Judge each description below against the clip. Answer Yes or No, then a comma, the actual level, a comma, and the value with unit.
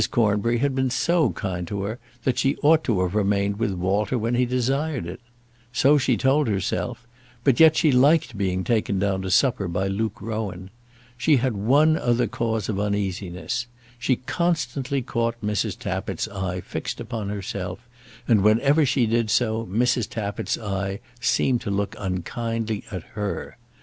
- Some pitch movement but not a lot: Yes, average, 4.3 semitones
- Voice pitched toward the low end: Yes, low, 110 Hz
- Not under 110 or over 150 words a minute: No, average, 165 wpm